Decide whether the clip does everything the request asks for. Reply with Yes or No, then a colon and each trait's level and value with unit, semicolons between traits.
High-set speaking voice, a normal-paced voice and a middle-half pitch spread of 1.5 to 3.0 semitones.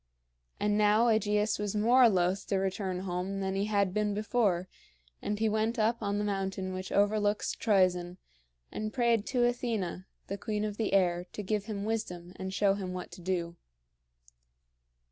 Yes: high, 205 Hz; average, 170 wpm; narrow, 2.4 semitones